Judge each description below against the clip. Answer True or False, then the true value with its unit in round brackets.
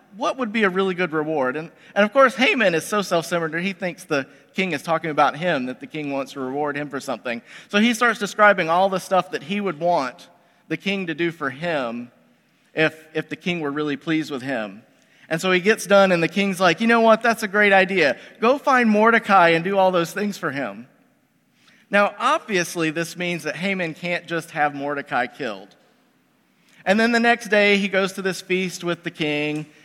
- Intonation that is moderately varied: True (4.4 semitones)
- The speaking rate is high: True (215 wpm)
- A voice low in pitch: False (180 Hz)